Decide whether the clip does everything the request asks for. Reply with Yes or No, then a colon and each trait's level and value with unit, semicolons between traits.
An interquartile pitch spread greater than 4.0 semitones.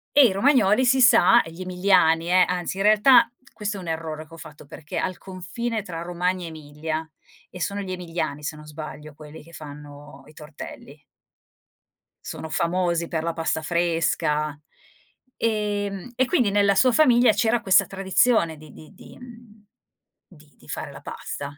Yes: average, 4.7 semitones